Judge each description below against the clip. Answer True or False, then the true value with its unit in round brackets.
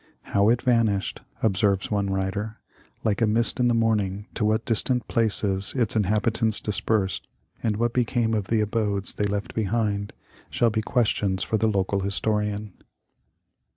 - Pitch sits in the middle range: False (105 Hz)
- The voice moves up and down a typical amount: False (2.1 semitones)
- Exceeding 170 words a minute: False (160 wpm)